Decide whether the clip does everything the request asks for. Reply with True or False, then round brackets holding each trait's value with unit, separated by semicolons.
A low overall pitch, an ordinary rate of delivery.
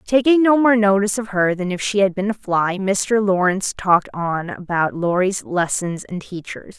False (195 Hz; 195 wpm)